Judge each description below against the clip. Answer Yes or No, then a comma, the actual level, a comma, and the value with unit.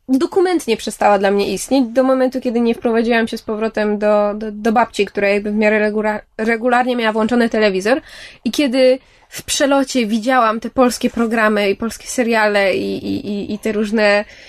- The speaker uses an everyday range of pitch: Yes, average, 3.0 semitones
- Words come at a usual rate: No, fast, 180 wpm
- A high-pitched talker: Yes, high, 225 Hz